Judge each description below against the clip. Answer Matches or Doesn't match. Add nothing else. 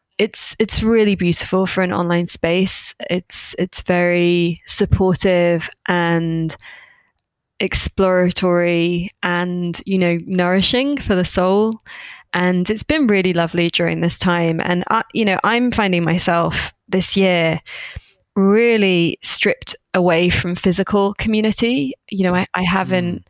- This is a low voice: Doesn't match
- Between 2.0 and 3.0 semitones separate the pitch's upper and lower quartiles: Matches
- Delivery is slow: Matches